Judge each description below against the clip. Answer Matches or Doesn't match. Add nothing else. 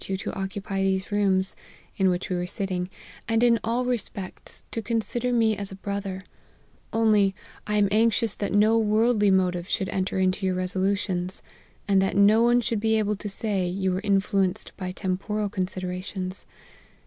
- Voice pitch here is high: Matches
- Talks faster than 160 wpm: Matches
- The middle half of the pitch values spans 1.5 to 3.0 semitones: Matches